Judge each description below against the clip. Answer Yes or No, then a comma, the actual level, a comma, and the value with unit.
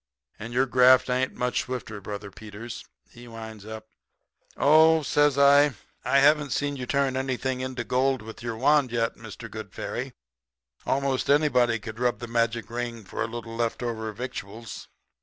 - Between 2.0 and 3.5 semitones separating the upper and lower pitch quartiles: Yes, average, 2.9 semitones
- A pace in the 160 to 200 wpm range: Yes, average, 165 wpm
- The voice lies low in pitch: Yes, low, 120 Hz